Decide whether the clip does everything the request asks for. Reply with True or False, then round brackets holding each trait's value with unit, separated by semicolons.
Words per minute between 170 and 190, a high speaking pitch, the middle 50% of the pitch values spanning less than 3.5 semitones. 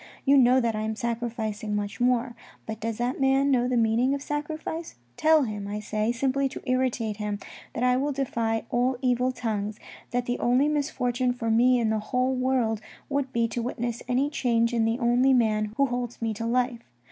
False (200 wpm; 245 Hz; 2.5 semitones)